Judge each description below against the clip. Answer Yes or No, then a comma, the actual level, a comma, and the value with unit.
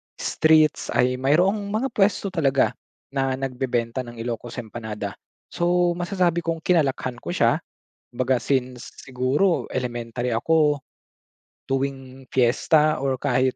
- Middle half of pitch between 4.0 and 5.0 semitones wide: Yes, average, 4.5 semitones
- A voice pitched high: No, low, 135 Hz